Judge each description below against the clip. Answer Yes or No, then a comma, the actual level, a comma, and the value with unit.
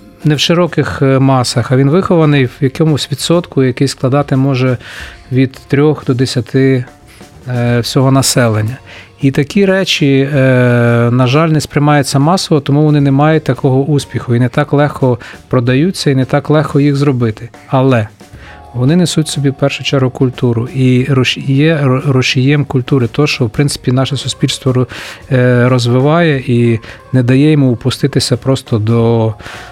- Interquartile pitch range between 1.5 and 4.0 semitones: Yes, narrow, 2.6 semitones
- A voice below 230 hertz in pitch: Yes, low, 135 Hz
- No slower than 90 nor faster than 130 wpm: No, average, 145 wpm